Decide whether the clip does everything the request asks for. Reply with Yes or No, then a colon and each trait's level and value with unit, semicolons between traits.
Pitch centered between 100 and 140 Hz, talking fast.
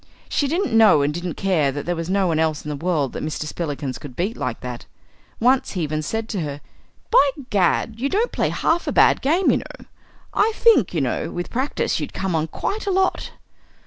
No: medium, 180 Hz; fast, 220 wpm